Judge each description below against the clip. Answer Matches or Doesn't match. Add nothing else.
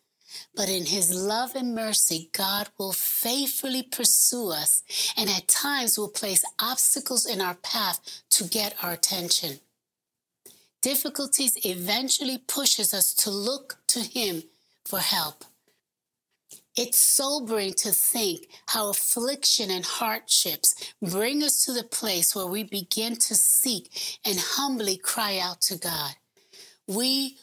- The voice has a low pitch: Doesn't match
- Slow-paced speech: Matches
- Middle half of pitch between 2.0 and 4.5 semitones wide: Doesn't match